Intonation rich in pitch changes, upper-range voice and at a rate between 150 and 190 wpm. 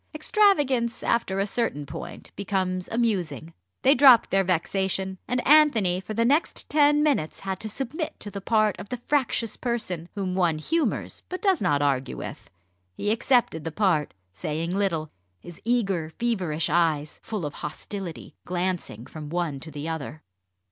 Yes: wide, 6.5 semitones; high, 195 Hz; average, 160 wpm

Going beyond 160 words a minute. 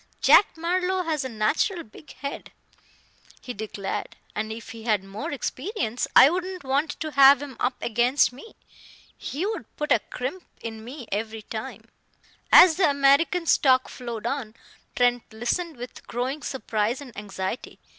No: average, 155 wpm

